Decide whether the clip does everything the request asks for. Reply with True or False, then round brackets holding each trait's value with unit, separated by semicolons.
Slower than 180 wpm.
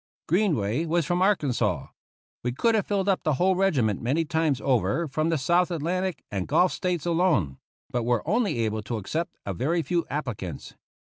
False (185 wpm)